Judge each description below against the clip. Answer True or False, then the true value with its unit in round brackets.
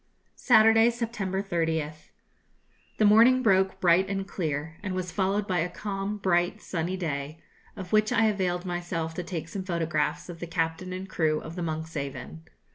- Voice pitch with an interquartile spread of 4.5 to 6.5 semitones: False (3.2 semitones)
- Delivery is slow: False (165 wpm)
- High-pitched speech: False (180 Hz)